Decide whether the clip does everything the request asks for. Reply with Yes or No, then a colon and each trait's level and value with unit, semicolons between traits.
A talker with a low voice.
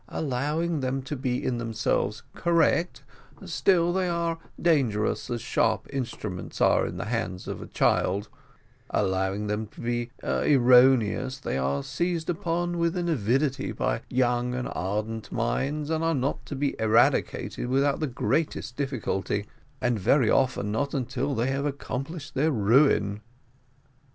Yes: low, 130 Hz